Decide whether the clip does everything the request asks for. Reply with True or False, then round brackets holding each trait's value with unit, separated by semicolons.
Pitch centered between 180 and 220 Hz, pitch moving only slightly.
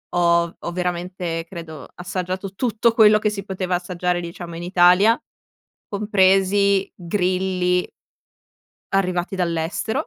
True (185 Hz; 2.1 semitones)